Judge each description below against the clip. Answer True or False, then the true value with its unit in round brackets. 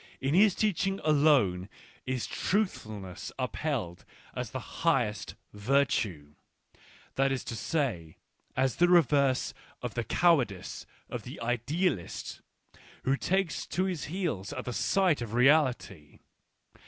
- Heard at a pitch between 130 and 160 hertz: True (135 Hz)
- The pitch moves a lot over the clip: True (7.7 semitones)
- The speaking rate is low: True (130 wpm)